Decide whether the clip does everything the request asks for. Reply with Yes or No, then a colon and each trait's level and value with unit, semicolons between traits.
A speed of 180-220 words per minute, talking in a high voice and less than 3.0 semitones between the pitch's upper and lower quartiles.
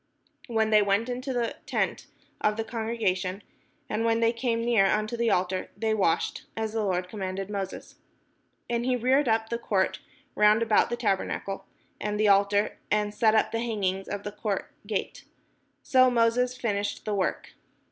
No: average, 170 wpm; high, 215 Hz; narrow, 2.5 semitones